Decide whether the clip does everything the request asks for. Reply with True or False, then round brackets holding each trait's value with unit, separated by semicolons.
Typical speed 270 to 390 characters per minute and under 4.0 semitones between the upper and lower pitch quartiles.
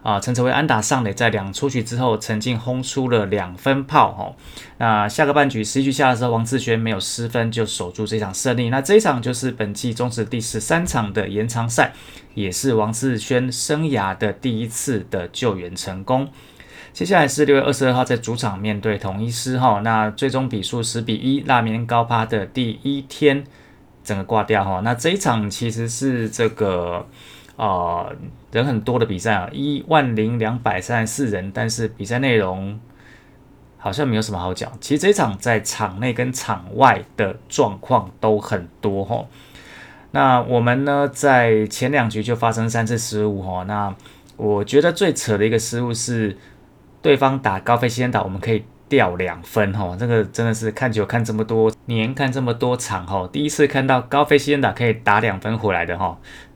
True (280 characters per minute; 3.4 semitones)